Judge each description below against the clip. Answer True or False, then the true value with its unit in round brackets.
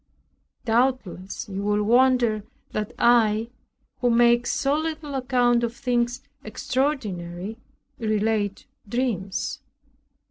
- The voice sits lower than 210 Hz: False (235 Hz)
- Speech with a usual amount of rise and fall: True (3.3 semitones)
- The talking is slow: True (95 wpm)